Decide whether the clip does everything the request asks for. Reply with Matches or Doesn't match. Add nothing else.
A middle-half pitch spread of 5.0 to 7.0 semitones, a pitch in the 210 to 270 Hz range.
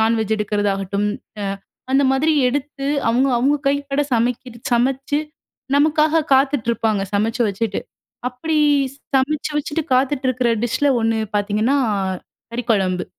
Doesn't match